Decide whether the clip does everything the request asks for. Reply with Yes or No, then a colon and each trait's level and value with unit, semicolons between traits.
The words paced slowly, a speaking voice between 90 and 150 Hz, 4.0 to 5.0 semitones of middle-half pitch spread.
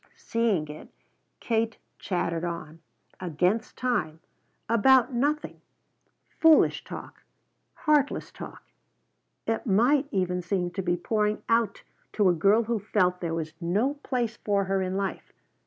No: slow, 130 wpm; high, 200 Hz; average, 4.6 semitones